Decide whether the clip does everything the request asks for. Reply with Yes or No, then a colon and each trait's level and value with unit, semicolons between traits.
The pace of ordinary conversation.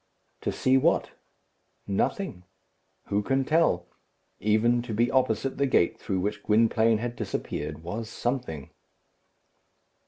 No: slow, 120 wpm